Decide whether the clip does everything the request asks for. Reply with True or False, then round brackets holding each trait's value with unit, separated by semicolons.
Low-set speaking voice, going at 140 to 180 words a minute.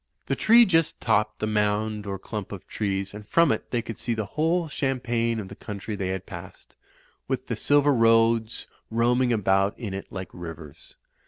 False (110 Hz; 190 wpm)